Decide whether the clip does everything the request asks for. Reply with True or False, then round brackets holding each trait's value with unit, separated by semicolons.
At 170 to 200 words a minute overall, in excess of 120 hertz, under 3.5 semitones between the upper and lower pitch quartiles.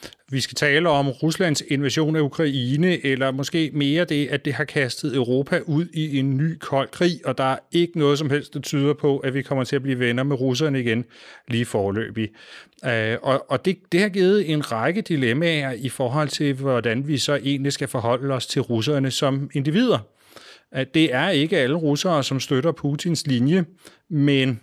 True (185 wpm; 140 Hz; 2.8 semitones)